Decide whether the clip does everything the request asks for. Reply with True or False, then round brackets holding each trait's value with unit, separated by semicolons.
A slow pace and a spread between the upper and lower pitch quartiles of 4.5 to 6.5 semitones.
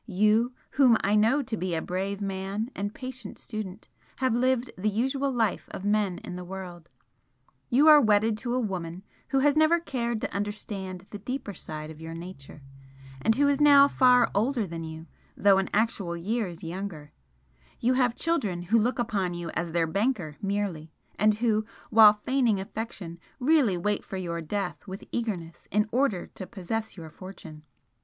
False (175 wpm; 4.9 semitones)